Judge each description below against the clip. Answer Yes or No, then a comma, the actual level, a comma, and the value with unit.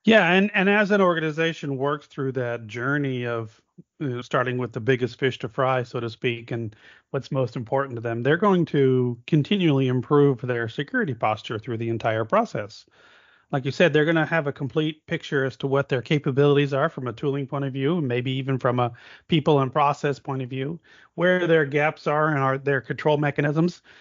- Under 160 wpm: No, fast, 205 wpm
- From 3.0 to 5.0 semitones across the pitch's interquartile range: Yes, average, 3.5 semitones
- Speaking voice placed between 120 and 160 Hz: Yes, medium, 140 Hz